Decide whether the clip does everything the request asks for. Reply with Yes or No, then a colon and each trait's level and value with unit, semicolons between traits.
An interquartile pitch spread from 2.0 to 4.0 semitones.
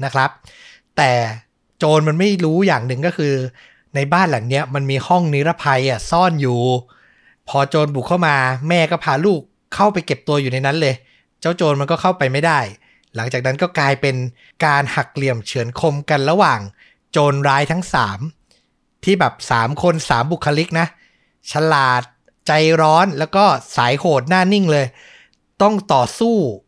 No: average, 4.4 semitones